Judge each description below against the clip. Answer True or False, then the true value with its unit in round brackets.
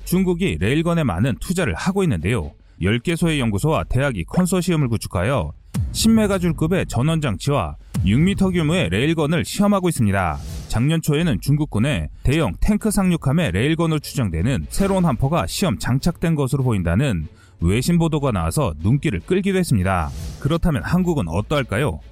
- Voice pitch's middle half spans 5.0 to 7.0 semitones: False (8.1 semitones)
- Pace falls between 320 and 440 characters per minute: True (370 characters per minute)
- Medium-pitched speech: True (145 Hz)